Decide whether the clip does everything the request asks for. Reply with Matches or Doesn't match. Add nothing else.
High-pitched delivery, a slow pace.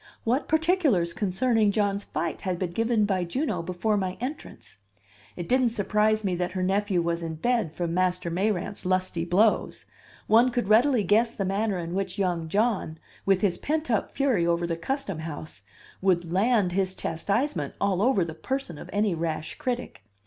Doesn't match